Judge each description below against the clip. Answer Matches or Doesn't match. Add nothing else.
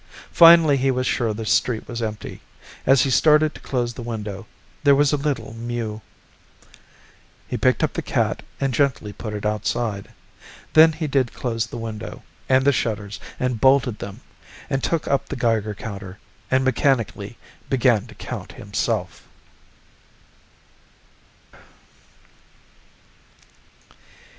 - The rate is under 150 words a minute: Matches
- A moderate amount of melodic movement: Matches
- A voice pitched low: Matches